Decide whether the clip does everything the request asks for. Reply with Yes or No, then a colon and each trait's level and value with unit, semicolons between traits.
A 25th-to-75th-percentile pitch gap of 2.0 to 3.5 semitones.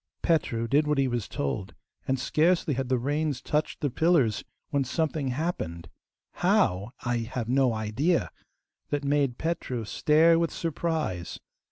No: average, 4.8 semitones